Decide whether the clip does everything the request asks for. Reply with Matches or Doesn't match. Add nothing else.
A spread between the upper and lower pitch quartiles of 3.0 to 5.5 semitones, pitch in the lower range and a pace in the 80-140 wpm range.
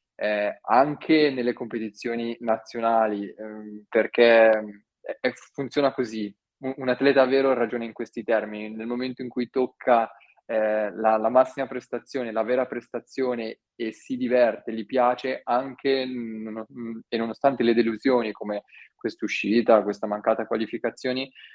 Doesn't match